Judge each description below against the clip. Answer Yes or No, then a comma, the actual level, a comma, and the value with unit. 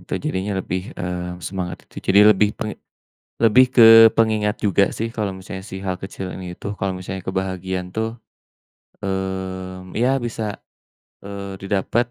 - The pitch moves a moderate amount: No, narrow, 1.9 semitones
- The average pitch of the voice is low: Yes, very low, 95 Hz